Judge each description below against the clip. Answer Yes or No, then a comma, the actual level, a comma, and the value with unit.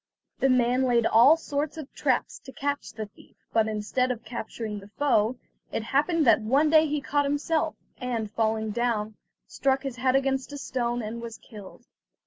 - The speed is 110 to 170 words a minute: No, average, 185 wpm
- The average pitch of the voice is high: Yes, very high, 250 Hz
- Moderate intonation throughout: Yes, average, 4.2 semitones